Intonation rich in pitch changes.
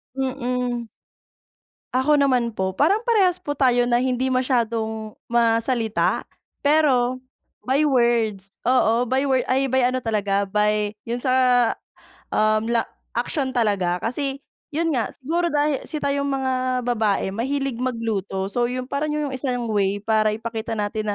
No: average, 3.4 semitones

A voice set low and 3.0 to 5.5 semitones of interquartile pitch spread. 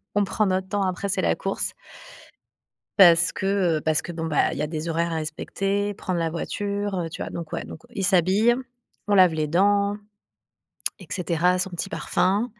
No: medium, 185 Hz; average, 3.4 semitones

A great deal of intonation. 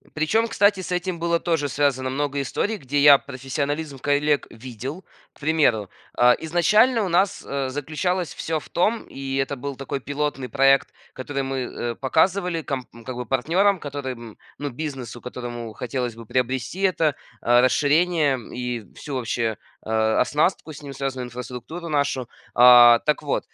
No: average, 4.2 semitones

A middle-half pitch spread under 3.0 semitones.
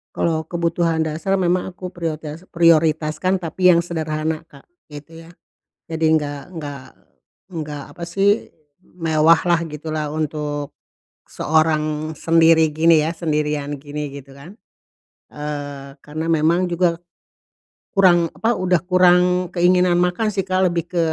Yes: narrow, 2.5 semitones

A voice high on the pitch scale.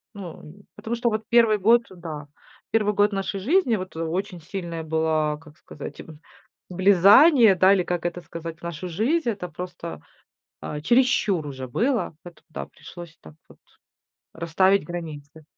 No: medium, 180 Hz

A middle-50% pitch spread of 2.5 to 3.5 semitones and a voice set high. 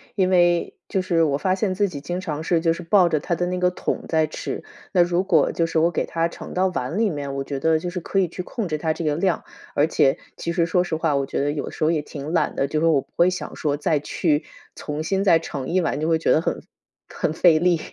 No: average, 2.9 semitones; medium, 165 Hz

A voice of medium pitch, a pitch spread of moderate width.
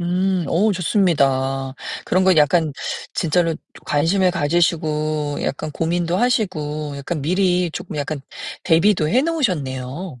Yes: medium, 165 Hz; average, 3.7 semitones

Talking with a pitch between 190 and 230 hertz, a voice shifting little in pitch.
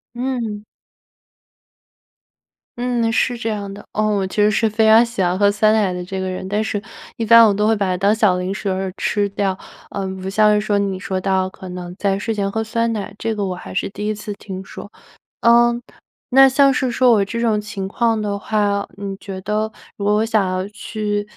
Yes: high, 205 Hz; narrow, 2.3 semitones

